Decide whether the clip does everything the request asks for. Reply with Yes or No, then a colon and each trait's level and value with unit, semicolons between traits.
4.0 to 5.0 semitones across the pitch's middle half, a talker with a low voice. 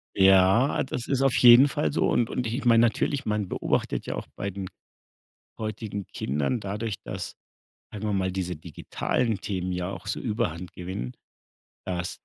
Yes: average, 4.3 semitones; low, 100 Hz